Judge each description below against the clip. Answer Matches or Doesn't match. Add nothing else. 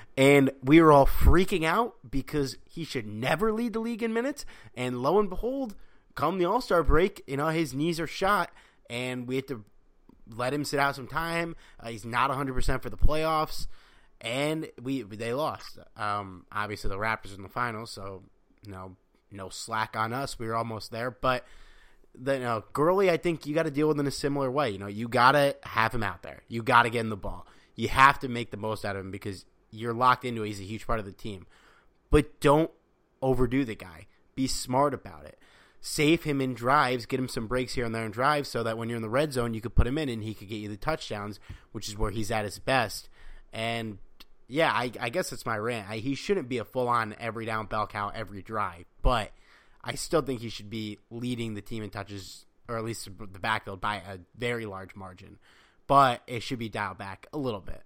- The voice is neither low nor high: Doesn't match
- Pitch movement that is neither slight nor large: Matches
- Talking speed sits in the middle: Doesn't match